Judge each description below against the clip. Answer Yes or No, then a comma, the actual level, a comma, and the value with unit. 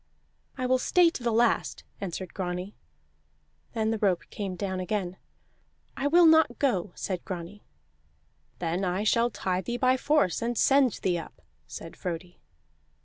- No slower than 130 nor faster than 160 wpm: Yes, average, 150 wpm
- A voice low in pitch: No, high, 205 Hz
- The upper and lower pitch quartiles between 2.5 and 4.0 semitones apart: No, average, 5.3 semitones